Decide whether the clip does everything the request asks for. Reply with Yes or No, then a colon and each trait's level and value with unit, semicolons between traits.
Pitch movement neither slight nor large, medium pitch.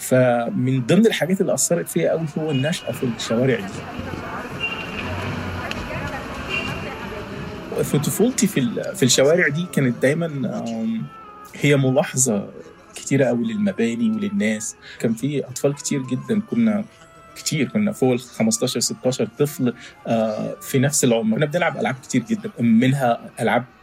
No: wide, 7.6 semitones; medium, 145 Hz